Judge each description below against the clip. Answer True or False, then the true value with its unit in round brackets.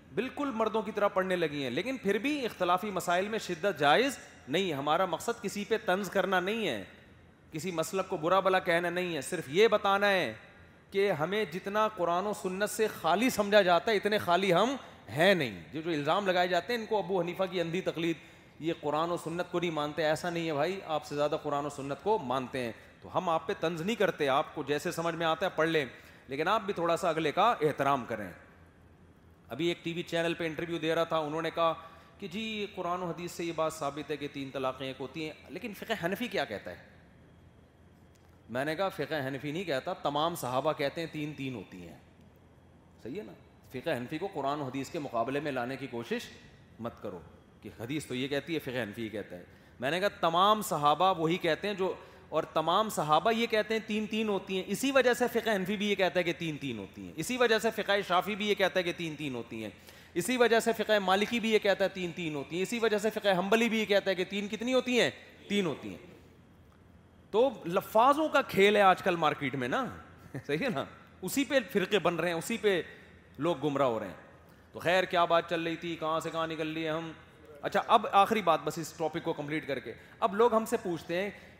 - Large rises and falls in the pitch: True (5.7 semitones)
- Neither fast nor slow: False (235 wpm)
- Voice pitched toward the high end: False (170 Hz)